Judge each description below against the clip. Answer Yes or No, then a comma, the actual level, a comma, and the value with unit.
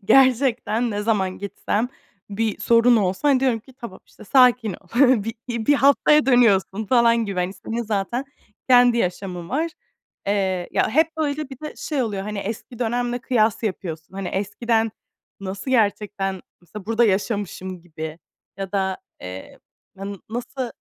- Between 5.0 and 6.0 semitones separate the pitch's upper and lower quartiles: No, average, 4.2 semitones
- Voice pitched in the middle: No, high, 220 Hz